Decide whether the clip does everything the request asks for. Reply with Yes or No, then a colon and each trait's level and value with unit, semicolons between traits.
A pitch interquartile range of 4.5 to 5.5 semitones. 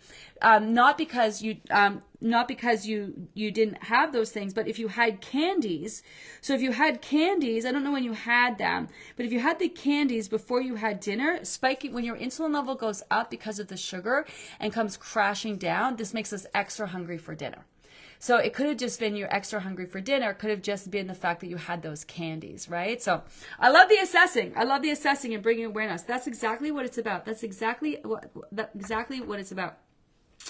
No: average, 4.1 semitones